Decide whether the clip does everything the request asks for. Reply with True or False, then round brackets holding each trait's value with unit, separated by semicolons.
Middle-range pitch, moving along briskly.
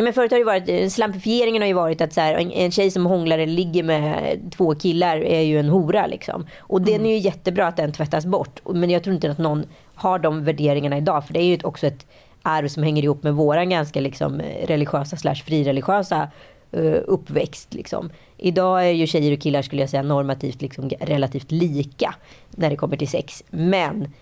True (160 Hz; 205 wpm)